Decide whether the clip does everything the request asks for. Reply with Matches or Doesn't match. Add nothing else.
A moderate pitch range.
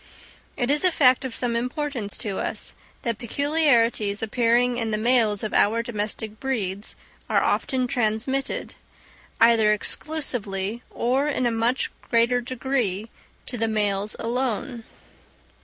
Matches